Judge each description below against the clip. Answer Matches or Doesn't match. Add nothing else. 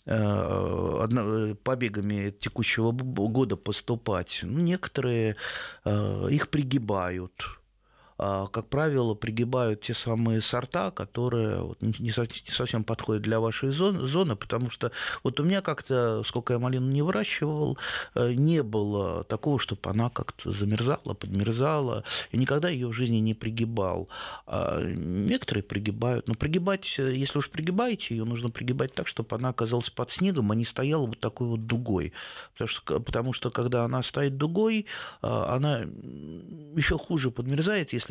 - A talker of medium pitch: Doesn't match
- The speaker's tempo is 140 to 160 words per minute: Doesn't match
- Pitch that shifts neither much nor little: Matches